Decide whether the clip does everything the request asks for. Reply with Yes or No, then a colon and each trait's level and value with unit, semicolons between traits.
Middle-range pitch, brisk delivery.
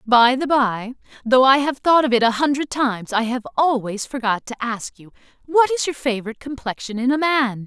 No: very high, 250 Hz; fast, 210 wpm